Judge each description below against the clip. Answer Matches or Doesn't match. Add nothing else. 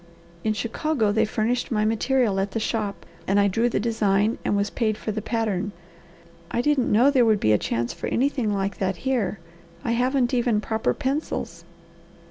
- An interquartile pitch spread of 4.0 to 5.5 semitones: Doesn't match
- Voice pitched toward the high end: Matches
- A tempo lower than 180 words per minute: Doesn't match